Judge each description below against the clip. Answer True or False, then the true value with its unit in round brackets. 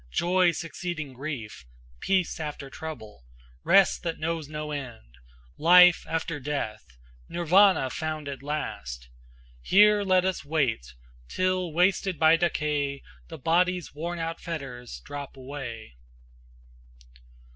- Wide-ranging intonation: False (4.3 semitones)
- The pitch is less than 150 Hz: False (155 Hz)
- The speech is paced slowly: True (115 wpm)